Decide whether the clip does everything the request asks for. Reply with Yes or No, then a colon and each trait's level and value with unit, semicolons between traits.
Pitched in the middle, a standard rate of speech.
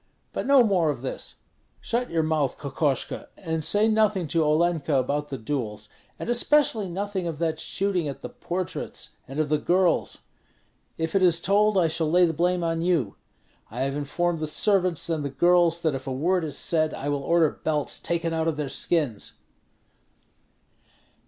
Yes: medium, 165 Hz; average, 180 wpm